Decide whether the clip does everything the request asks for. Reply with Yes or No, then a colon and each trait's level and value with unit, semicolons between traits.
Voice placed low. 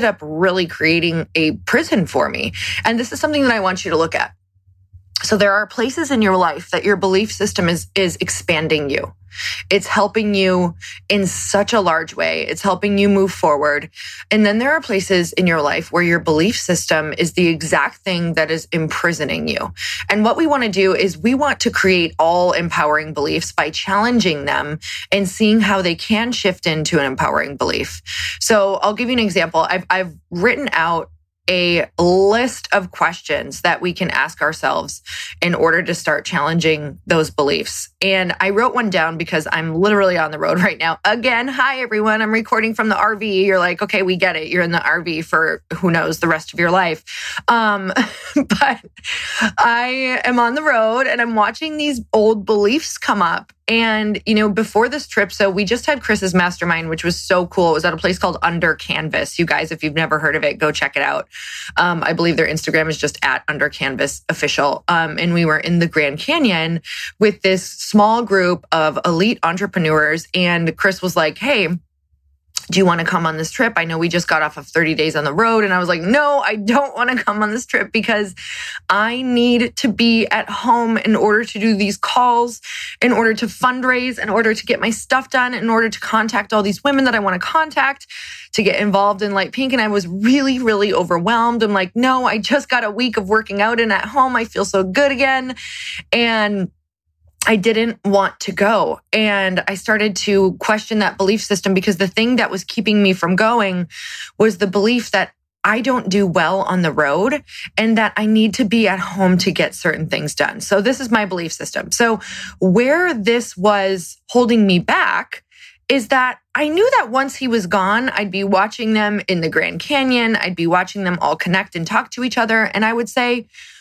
No: high, 200 Hz